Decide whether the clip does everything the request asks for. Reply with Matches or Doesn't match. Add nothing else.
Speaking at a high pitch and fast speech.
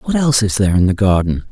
Doesn't match